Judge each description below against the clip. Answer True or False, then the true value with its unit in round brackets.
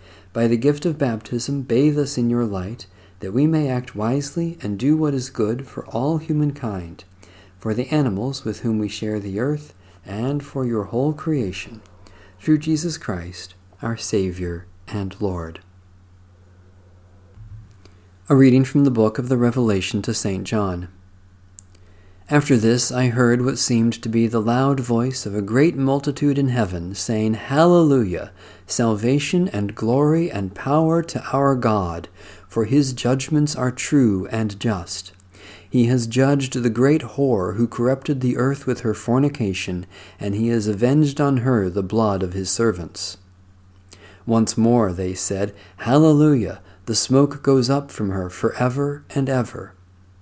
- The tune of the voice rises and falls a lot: True (6.1 semitones)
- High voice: False (115 Hz)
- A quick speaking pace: False (155 wpm)